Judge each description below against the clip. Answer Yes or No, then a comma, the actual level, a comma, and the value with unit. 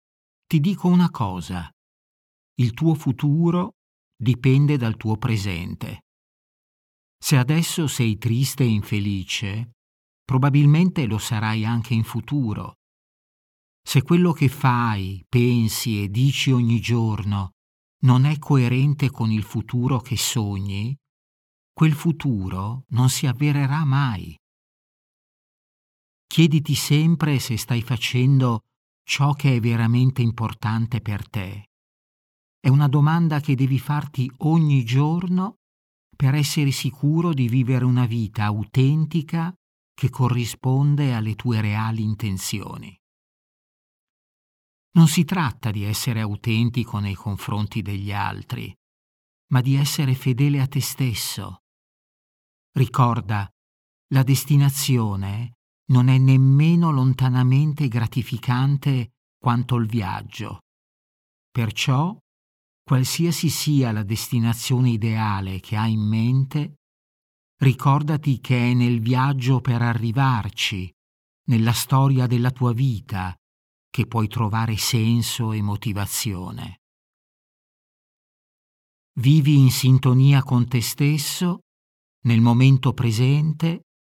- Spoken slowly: Yes, slow, 105 wpm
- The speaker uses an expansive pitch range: No, average, 4.4 semitones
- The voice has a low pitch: Yes, low, 125 Hz